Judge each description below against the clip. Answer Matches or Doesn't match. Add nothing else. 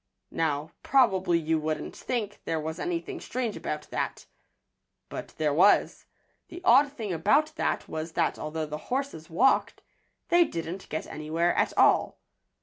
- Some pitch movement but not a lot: Doesn't match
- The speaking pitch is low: Doesn't match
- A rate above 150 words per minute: Doesn't match